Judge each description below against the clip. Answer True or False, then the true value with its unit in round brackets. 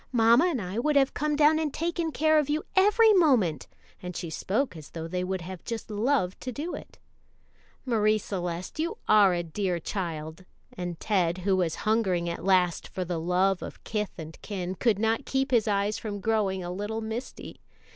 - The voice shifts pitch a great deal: True (6.2 semitones)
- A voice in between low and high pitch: False (205 Hz)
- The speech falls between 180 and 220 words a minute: True (195 wpm)